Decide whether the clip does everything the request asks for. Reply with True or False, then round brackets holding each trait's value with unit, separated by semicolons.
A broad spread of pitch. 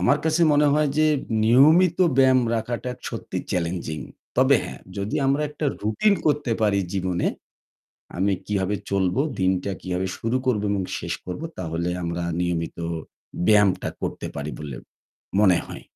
True (6.6 semitones)